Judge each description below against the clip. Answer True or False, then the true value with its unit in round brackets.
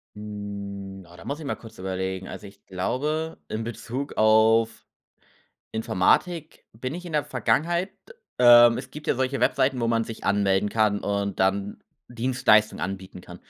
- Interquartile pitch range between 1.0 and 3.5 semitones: False (4.6 semitones)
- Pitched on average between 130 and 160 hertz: False (110 Hz)